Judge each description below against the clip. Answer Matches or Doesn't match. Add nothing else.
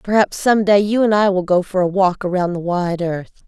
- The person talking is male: Doesn't match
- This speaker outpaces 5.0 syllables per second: Doesn't match